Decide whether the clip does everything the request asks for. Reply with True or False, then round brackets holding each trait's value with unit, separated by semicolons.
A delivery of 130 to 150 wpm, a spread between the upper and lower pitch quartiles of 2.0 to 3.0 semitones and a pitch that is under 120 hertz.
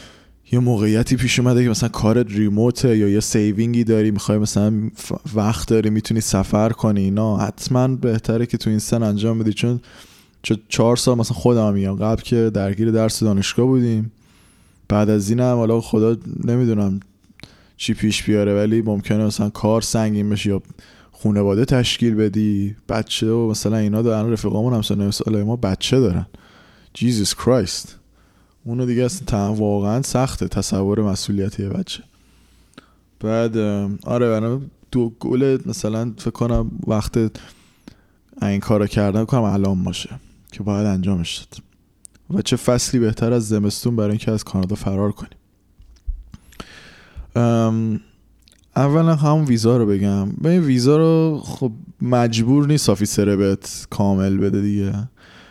True (140 wpm; 2.7 semitones; 110 Hz)